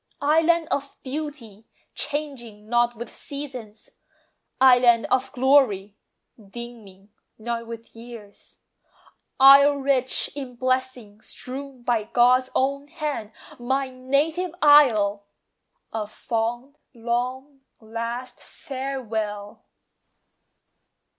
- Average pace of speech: No, slow, 90 wpm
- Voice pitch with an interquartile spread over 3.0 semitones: Yes, average, 3.5 semitones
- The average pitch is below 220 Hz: No, very high, 250 Hz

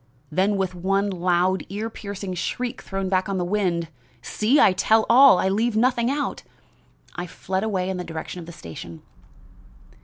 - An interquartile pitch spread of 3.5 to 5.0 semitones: No, average, 2.9 semitones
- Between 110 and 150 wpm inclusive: No, average, 175 wpm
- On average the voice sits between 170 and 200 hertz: Yes, high, 190 Hz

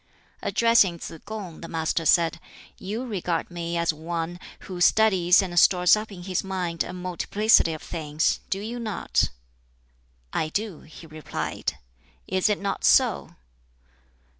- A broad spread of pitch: No, average, 3.2 semitones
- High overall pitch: No, medium, 180 Hz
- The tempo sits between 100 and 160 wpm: Yes, average, 140 wpm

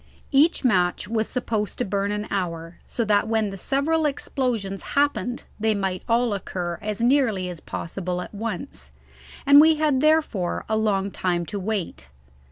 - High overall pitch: Yes, high, 210 Hz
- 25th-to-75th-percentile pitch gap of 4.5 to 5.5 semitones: Yes, average, 5.1 semitones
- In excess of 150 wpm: Yes, average, 165 wpm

